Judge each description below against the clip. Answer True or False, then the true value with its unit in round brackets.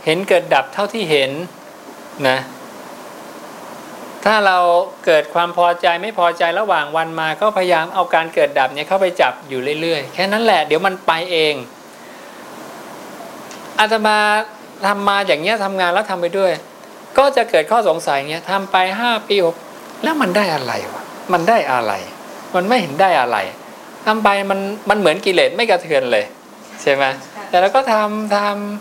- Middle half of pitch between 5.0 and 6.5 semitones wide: False (4.4 semitones)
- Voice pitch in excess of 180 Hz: True (190 Hz)